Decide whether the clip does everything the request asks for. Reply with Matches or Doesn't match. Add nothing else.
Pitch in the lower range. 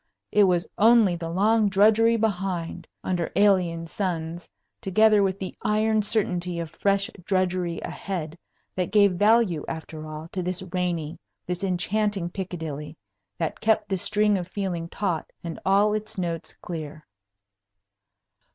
Doesn't match